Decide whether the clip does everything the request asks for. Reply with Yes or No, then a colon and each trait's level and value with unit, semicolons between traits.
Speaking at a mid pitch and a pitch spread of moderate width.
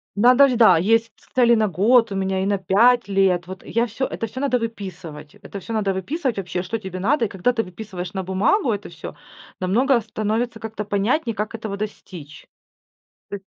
No: high, 210 Hz; average, 3.6 semitones